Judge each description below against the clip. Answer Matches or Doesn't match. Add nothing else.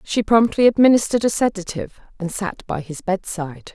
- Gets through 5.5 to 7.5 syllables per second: Matches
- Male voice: Doesn't match